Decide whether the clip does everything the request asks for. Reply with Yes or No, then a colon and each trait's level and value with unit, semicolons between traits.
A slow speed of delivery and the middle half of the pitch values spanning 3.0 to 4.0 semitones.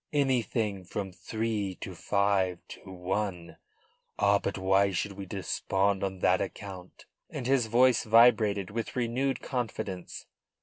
Yes: slow, 130 wpm; average, 3.3 semitones